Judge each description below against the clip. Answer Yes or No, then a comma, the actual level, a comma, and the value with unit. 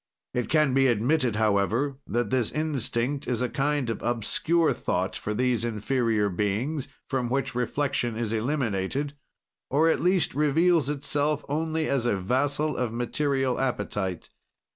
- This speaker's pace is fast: No, average, 140 wpm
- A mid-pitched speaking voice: No, low, 130 Hz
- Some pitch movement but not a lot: Yes, average, 4.3 semitones